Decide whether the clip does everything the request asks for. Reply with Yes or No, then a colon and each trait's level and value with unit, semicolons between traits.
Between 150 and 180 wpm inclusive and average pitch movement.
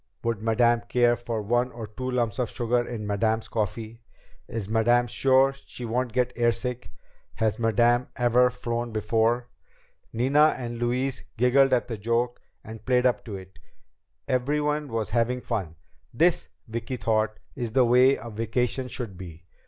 No: average, 155 wpm; narrow, 2.0 semitones